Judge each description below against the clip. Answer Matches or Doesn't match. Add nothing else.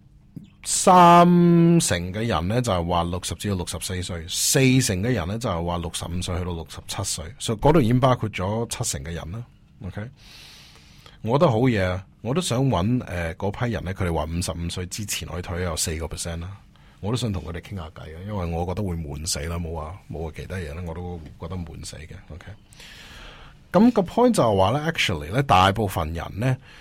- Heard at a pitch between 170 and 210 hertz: Doesn't match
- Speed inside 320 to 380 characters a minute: Matches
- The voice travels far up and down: Matches